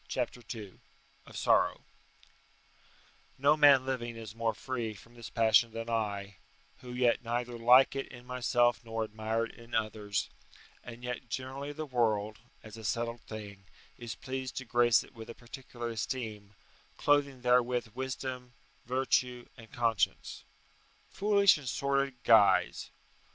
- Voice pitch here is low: Yes, low, 120 Hz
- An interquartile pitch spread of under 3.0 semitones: Yes, narrow, 2.5 semitones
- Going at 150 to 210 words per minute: No, average, 140 wpm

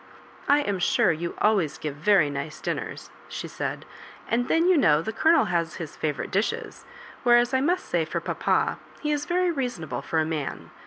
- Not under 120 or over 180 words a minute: No, average, 200 wpm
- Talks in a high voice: Yes, high, 205 Hz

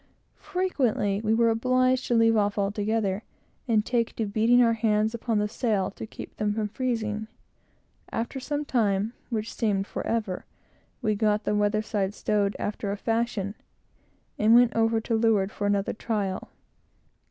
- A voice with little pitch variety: Yes, narrow, 1.9 semitones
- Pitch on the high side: Yes, high, 220 Hz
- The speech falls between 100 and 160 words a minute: Yes, average, 155 wpm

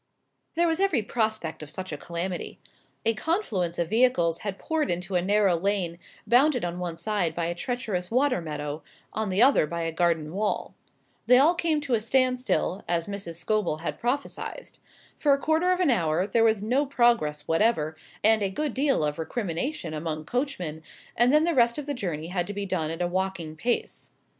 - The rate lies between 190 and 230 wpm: Yes, average, 195 wpm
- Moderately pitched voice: No, high, 200 Hz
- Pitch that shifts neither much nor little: No, wide, 6.9 semitones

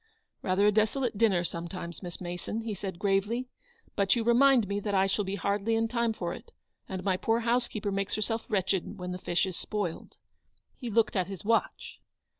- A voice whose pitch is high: Yes, high, 205 Hz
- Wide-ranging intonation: No, average, 3.2 semitones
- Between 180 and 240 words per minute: Yes, average, 200 wpm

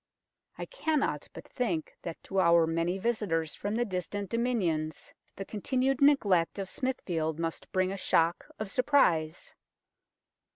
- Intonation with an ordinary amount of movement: No, wide, 6.2 semitones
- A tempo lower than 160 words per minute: Yes, slow, 135 wpm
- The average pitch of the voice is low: No, high, 190 Hz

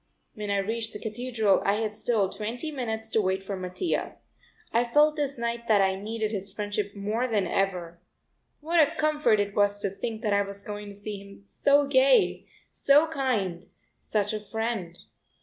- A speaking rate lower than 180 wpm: No, average, 185 wpm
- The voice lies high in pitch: Yes, high, 215 Hz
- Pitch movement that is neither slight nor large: Yes, average, 3.3 semitones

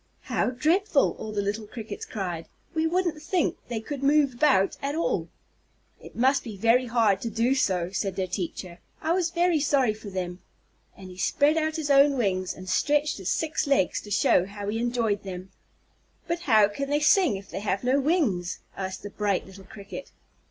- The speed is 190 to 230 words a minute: Yes, average, 195 wpm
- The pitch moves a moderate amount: No, wide, 7.0 semitones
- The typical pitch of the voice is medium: No, high, 230 Hz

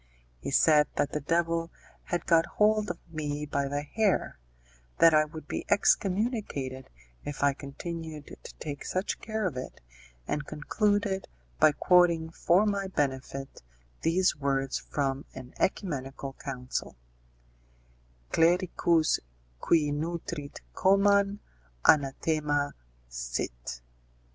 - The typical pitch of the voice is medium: Yes, medium, 155 Hz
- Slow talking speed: Yes, slow, 115 wpm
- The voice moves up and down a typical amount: Yes, average, 4.4 semitones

